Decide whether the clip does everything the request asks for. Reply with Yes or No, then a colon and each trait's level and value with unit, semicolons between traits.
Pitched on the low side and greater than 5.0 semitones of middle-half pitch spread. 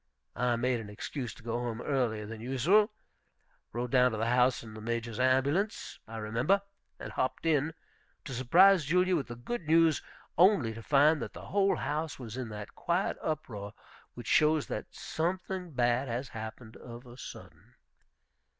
Yes: low, 130 Hz; wide, 5.4 semitones